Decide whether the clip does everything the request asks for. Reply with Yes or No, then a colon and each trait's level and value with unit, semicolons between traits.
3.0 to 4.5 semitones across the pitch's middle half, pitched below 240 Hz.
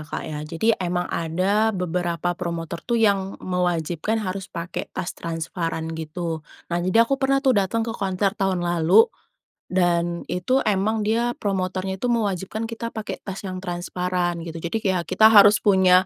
Yes: average, 3.4 semitones; medium, 185 Hz